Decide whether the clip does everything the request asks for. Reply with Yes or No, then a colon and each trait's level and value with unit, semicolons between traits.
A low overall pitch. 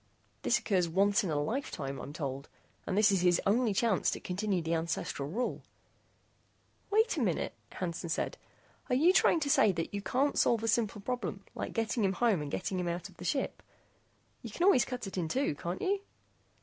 No: high, 195 Hz